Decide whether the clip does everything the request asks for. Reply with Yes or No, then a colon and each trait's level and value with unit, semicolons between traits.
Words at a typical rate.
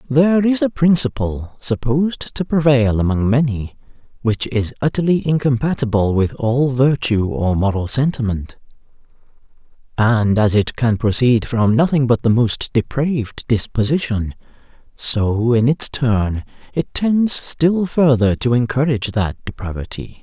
No: slow, 130 wpm